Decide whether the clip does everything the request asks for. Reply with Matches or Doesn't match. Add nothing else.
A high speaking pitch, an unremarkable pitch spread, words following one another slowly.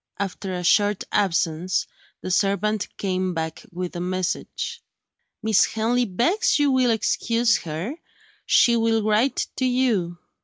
Matches